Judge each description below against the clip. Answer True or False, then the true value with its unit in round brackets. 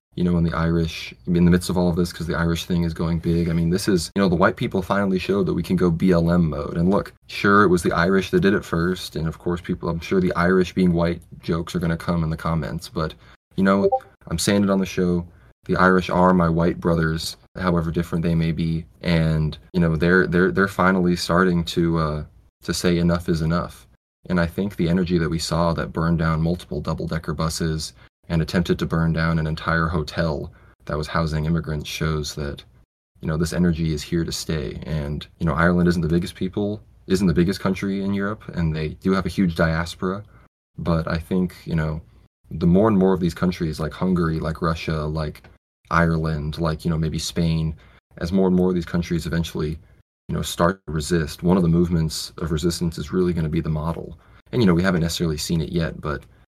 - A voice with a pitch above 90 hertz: False (85 Hz)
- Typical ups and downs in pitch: False (2.0 semitones)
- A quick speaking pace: True (225 wpm)